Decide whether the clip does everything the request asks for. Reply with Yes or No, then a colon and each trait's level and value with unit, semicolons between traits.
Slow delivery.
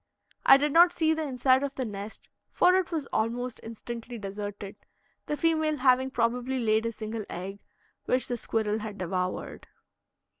No: average, 160 wpm